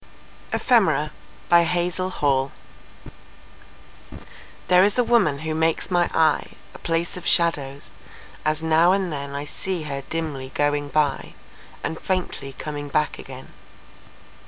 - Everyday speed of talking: No, slow, 125 wpm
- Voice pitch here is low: No, medium, 160 Hz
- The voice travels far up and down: No, average, 3.3 semitones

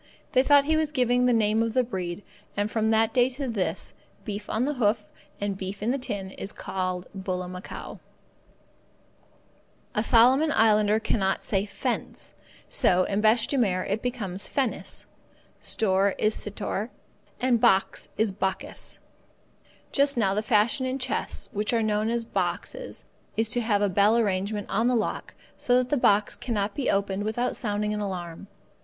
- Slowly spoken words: No, average, 165 wpm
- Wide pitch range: No, average, 3.4 semitones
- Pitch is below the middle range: No, high, 215 Hz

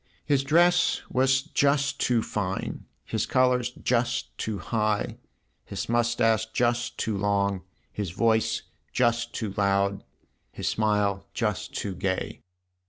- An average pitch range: Yes, average, 3.6 semitones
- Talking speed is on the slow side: Yes, slow, 120 wpm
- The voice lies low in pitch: Yes, low, 115 Hz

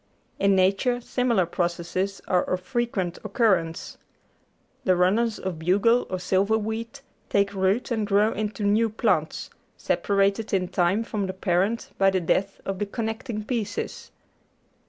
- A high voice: Yes, high, 200 Hz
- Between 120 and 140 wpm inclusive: Yes, slow, 135 wpm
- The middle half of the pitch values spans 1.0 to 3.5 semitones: Yes, average, 3.0 semitones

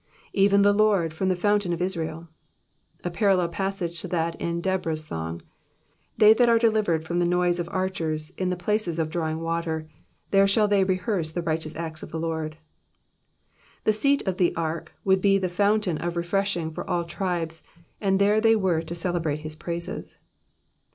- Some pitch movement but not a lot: Yes, average, 3.1 semitones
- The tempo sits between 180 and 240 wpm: Yes, average, 185 wpm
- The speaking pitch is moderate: Yes, medium, 175 Hz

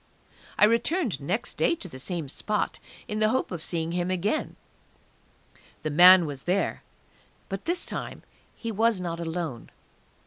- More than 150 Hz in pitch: Yes, medium, 185 Hz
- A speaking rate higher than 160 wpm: No, average, 150 wpm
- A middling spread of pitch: Yes, average, 4.5 semitones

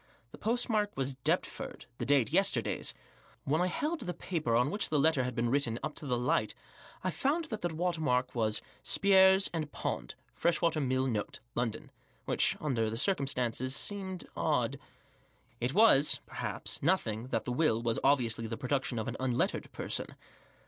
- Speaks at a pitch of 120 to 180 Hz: Yes, medium, 140 Hz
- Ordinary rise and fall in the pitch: No, wide, 6.6 semitones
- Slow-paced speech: No, average, 165 wpm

